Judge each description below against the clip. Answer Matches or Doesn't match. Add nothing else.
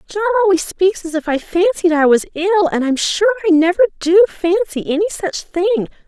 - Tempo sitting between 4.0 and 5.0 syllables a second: Doesn't match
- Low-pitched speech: Doesn't match